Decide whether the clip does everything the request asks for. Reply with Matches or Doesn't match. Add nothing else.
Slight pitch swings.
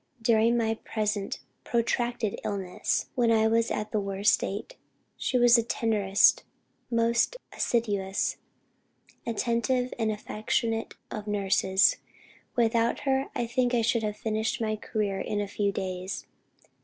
Matches